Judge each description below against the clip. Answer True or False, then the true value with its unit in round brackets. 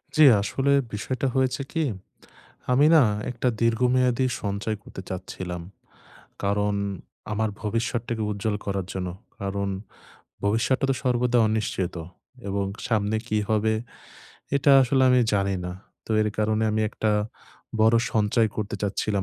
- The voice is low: True (110 Hz)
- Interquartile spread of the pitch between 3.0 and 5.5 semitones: True (3.6 semitones)